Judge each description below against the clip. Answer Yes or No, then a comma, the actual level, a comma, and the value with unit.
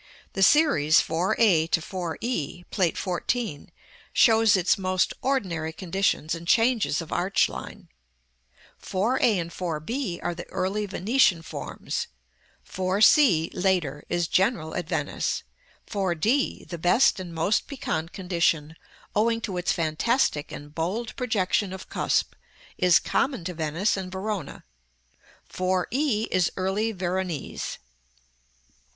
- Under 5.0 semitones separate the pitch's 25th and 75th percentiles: Yes, average, 4.3 semitones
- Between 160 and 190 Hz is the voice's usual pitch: Yes, medium, 185 Hz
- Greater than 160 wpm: No, slow, 135 wpm